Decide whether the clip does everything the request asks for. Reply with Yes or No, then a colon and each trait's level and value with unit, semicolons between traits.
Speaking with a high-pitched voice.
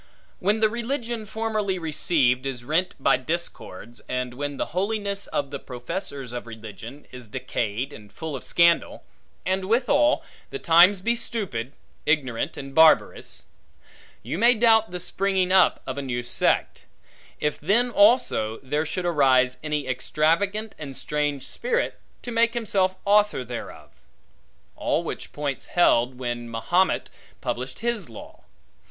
No: medium, 155 Hz